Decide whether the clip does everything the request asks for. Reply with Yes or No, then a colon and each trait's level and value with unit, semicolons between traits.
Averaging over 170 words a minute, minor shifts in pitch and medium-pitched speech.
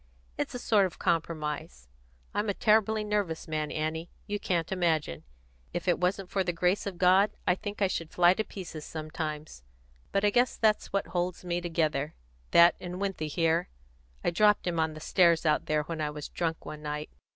No: average, 195 wpm; average, 3.8 semitones; medium, 175 Hz